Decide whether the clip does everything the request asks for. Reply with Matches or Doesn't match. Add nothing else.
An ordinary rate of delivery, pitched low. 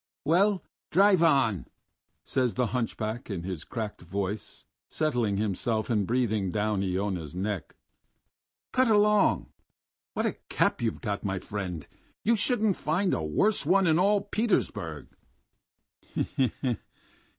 Doesn't match